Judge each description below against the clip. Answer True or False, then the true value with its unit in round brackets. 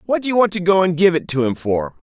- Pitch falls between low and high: True (175 Hz)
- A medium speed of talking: False (320 wpm)